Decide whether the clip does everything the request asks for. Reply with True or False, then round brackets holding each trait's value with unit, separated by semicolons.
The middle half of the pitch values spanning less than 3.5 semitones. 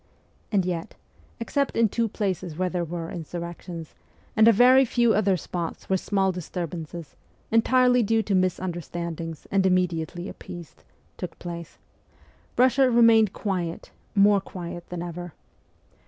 False (4.2 semitones)